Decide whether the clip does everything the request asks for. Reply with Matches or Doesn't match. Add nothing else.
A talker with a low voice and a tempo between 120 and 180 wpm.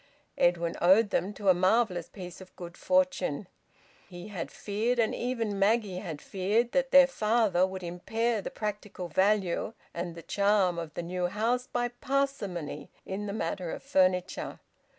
Doesn't match